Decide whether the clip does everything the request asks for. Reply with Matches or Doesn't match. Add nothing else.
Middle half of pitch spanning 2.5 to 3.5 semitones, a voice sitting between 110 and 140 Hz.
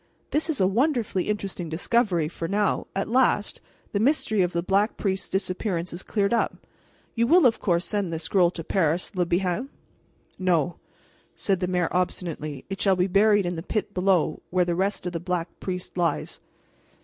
Doesn't match